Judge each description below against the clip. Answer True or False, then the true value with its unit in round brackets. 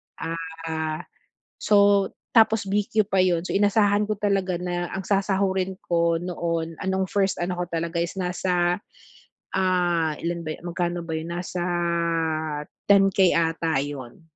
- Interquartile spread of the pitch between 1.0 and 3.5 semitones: True (2.5 semitones)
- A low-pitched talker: False (180 Hz)